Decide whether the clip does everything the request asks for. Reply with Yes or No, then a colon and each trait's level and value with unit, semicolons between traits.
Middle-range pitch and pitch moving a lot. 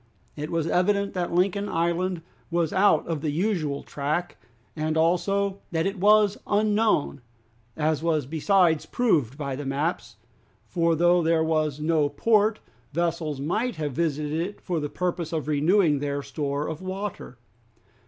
No: medium, 165 Hz; average, 3.8 semitones